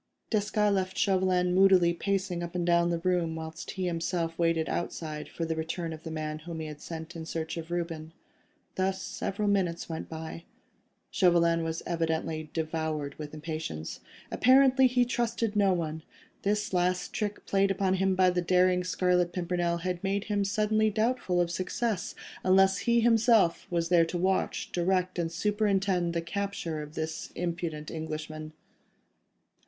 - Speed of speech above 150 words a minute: Yes, average, 160 wpm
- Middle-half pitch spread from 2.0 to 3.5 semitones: Yes, average, 2.9 semitones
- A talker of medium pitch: Yes, medium, 175 Hz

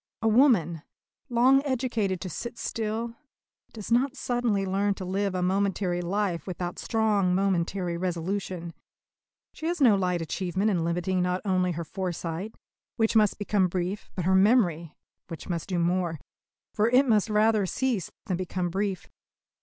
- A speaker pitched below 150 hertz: No, high, 190 Hz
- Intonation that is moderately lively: Yes, average, 3.6 semitones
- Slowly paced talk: No, average, 155 wpm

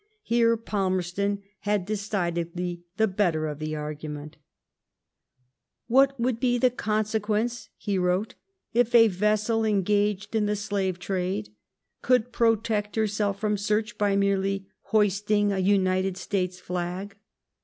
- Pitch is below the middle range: No, high, 205 Hz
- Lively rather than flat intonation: No, average, 2.7 semitones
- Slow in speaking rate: Yes, slow, 130 wpm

